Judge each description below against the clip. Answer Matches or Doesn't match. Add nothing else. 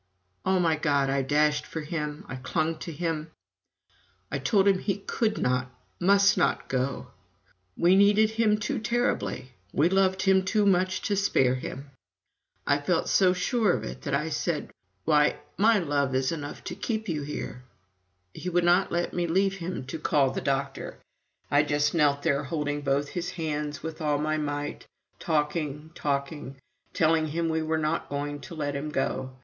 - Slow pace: Doesn't match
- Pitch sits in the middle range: Matches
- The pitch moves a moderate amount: Matches